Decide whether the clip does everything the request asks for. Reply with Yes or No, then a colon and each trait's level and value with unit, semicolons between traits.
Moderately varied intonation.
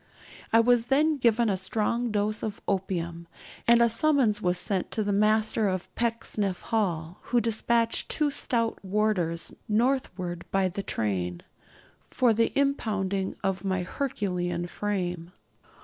Yes: average, 4.0 semitones